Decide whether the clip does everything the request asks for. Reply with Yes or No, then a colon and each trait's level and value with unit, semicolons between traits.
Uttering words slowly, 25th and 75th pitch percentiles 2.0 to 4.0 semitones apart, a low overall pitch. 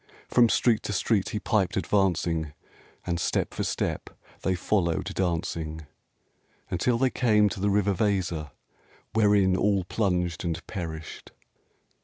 Yes: slow, 130 wpm; average, 3.4 semitones; very low, 95 Hz